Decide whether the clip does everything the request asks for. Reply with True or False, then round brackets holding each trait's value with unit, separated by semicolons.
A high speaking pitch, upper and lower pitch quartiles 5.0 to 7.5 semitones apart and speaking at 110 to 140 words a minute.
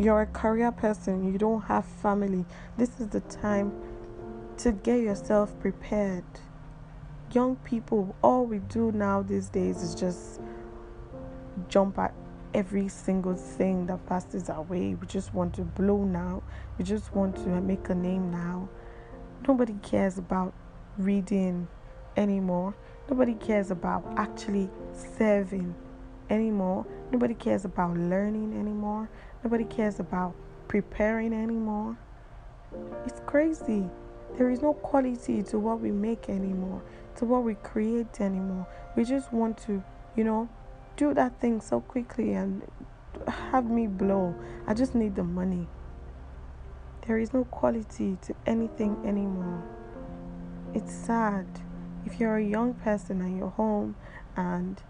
False (195 Hz; 4.2 semitones; 135 wpm)